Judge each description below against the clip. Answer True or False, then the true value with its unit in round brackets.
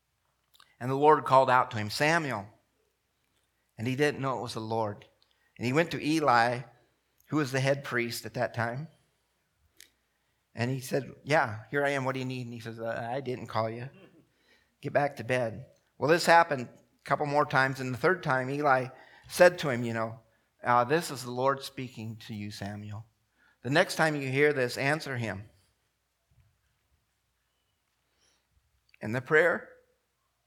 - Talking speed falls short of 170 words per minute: False (175 wpm)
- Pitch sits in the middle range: False (130 Hz)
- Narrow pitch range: False (4.1 semitones)